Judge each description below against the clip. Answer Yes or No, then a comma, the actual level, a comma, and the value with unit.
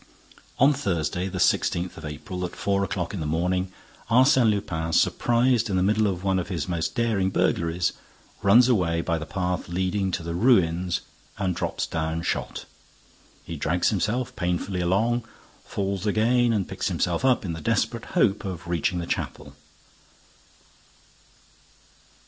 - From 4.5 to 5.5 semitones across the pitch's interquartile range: No, average, 3.8 semitones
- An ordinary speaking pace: Yes, average, 155 wpm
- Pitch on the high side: No, very low, 95 Hz